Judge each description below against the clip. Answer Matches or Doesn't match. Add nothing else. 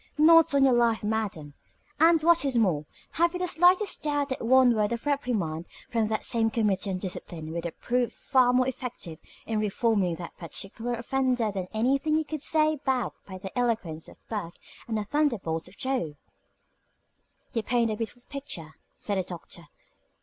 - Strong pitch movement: Matches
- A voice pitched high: Matches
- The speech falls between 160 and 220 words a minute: Matches